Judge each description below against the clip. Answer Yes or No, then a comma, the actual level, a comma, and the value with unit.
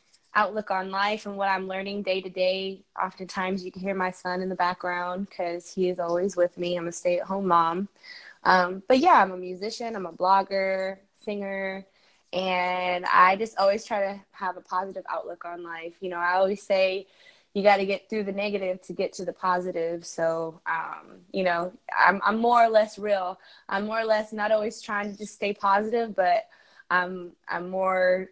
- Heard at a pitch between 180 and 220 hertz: Yes, high, 190 Hz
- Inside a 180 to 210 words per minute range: Yes, average, 200 wpm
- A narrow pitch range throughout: Yes, narrow, 1.9 semitones